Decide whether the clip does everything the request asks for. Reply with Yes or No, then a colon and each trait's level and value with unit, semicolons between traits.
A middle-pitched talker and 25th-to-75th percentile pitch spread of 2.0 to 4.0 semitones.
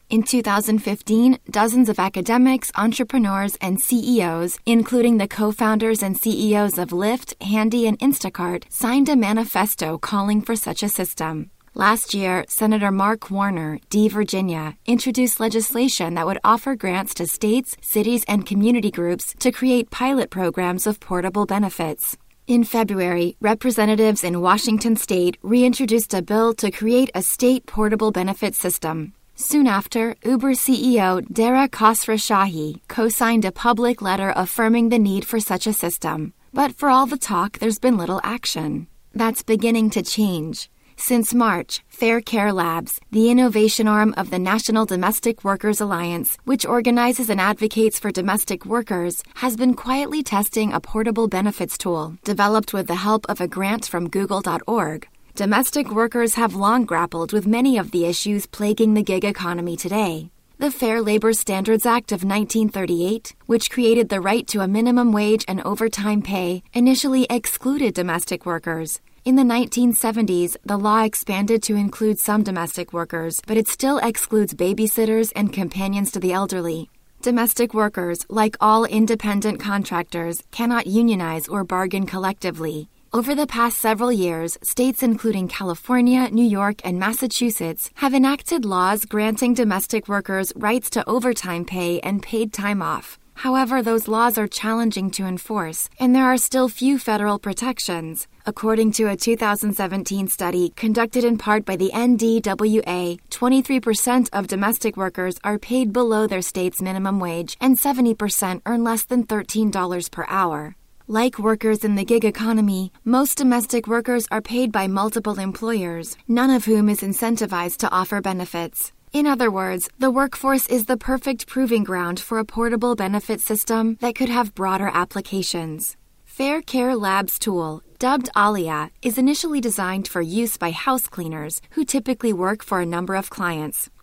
No: high, 215 Hz; average, 3.7 semitones